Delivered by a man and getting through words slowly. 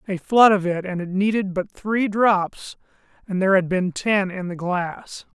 No: male; average, 190 wpm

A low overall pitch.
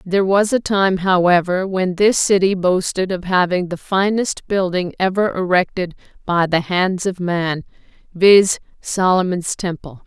No: medium, 185 Hz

